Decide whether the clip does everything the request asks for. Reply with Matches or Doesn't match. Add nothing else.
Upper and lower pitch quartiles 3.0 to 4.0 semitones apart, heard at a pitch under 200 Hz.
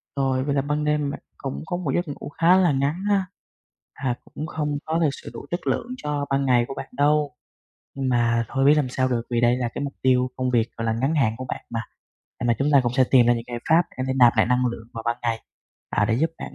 Matches